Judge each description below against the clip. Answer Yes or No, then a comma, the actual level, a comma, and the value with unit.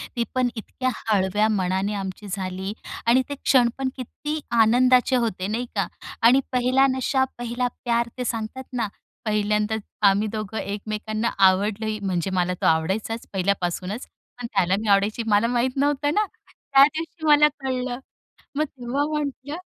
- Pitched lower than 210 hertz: No, high, 225 Hz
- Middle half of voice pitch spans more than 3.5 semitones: Yes, average, 4.1 semitones